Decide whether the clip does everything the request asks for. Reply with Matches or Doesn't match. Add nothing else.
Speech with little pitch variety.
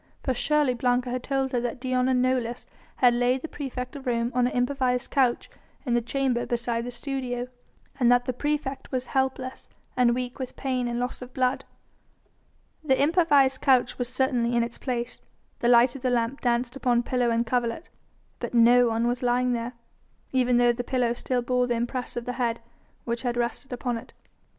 Matches